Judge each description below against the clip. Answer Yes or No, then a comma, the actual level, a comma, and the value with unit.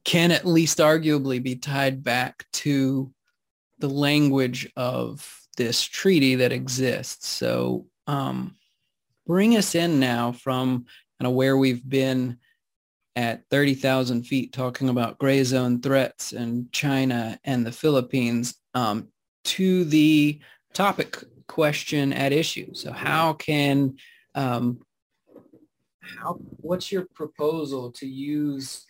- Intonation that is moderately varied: Yes, average, 3.1 semitones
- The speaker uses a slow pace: Yes, slow, 120 wpm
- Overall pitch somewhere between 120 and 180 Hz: Yes, low, 135 Hz